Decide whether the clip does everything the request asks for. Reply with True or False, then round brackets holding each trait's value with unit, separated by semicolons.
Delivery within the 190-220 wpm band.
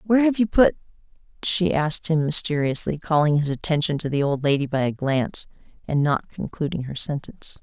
False (180 wpm)